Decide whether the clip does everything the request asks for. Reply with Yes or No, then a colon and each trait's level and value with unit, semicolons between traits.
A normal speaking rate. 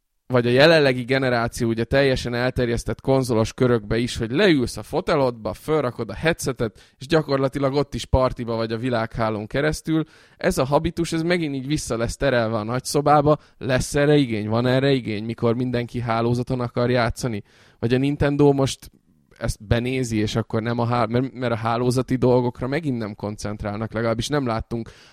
No: fast, 160 wpm